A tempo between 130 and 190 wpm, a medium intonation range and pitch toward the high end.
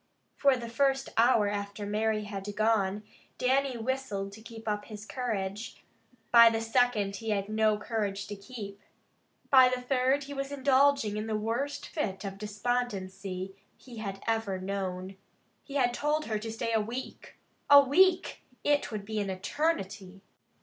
Yes: average, 160 wpm; average, 4.1 semitones; high, 220 Hz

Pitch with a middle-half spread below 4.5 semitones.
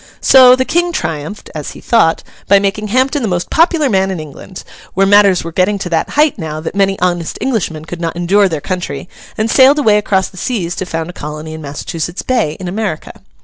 No: average, 5.0 semitones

